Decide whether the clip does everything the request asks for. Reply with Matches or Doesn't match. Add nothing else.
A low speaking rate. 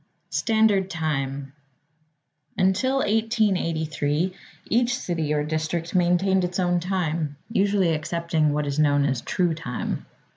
Matches